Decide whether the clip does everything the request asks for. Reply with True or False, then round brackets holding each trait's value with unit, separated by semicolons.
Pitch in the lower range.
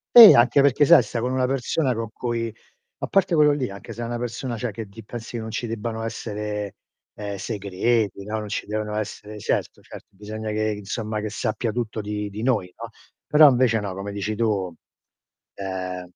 True (110 Hz)